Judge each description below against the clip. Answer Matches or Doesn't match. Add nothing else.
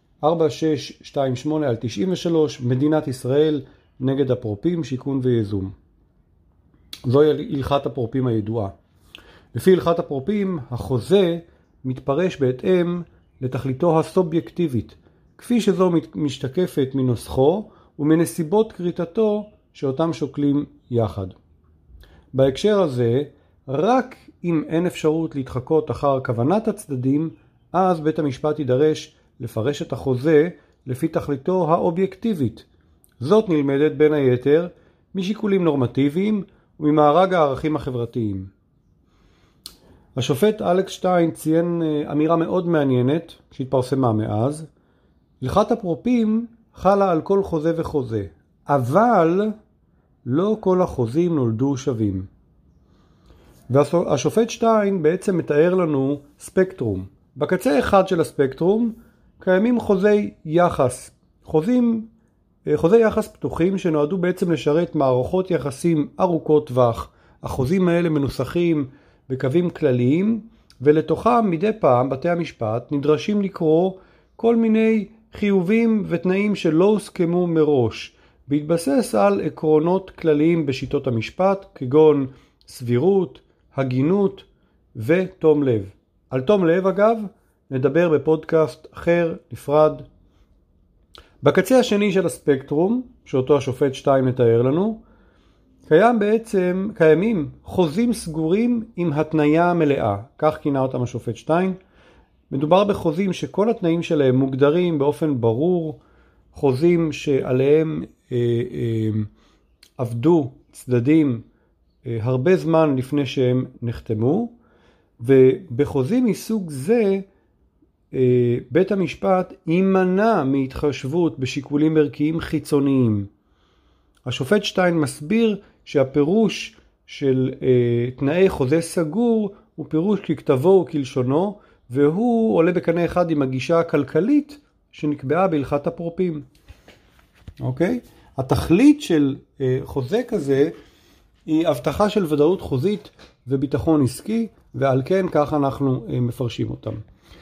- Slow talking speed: Matches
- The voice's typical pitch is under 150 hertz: Doesn't match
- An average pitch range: Doesn't match